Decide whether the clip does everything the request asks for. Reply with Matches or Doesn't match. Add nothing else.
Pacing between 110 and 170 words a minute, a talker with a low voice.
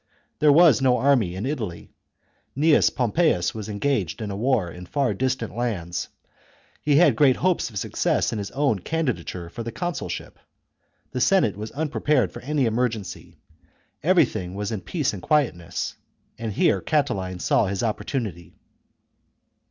Matches